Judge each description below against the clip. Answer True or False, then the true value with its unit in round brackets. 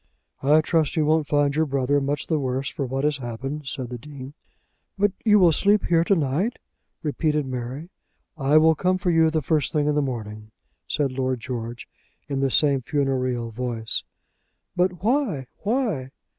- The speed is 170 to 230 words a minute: True (175 wpm)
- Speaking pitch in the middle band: True (145 Hz)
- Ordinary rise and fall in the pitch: True (3.8 semitones)